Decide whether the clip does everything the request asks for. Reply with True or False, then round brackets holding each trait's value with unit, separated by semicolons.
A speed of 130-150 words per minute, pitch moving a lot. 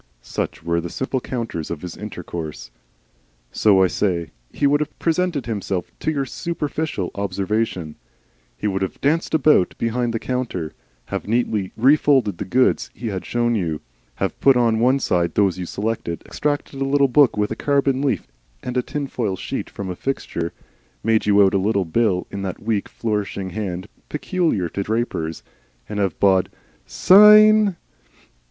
False (165 wpm; 6.4 semitones)